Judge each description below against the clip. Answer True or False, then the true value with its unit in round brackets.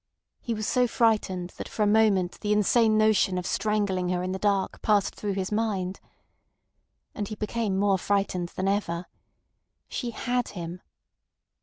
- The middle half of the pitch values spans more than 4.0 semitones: False (2.6 semitones)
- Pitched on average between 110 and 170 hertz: False (205 Hz)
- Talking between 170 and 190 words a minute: False (160 wpm)